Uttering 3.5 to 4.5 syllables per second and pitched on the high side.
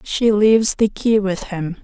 Yes: 4.1 syllables/s; high, 205 Hz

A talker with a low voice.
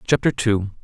Yes: low, 110 Hz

